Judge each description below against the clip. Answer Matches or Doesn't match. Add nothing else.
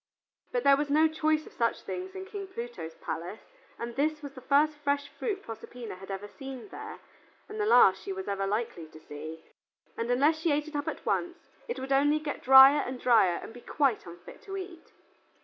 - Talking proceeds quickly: Matches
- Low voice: Doesn't match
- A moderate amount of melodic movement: Doesn't match